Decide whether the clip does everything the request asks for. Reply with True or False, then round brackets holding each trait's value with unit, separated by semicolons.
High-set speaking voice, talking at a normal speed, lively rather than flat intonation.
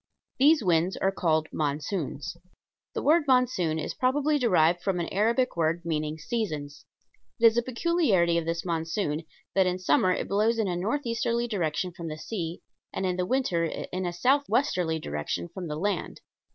False (180 Hz; 170 wpm; 6.2 semitones)